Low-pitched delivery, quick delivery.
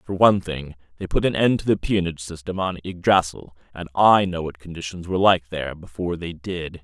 Yes: very low, 85 Hz; fast, 210 wpm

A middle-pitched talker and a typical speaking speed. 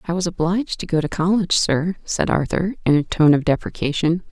No: medium, 170 Hz; fast, 210 wpm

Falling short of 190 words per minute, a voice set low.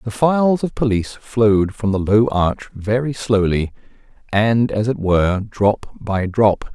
Yes: average, 160 wpm; low, 110 Hz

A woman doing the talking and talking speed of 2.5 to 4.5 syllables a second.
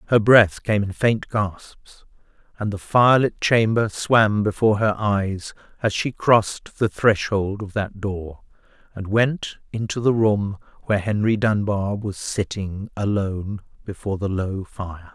No: male; 4.1 syllables/s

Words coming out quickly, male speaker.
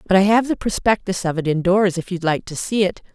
No: fast, 265 wpm; female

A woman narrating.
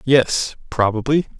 No: male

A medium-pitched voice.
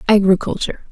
No: high, 200 Hz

